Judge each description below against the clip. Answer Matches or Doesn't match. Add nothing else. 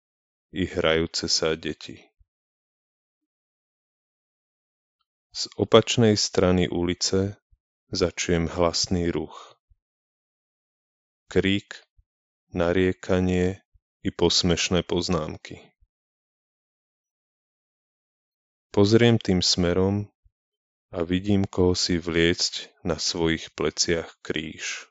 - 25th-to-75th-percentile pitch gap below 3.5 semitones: Matches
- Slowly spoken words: Matches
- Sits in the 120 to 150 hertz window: Doesn't match